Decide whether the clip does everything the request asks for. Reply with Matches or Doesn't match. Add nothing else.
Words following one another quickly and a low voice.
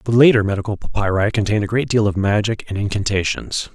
Doesn't match